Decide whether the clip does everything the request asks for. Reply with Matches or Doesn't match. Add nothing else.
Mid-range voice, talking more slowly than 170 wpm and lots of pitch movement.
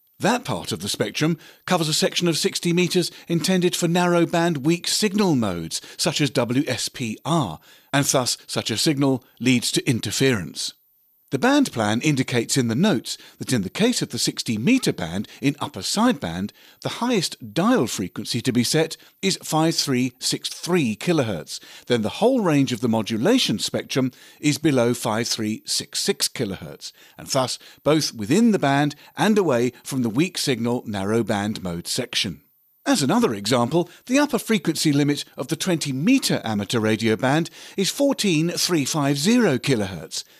Matches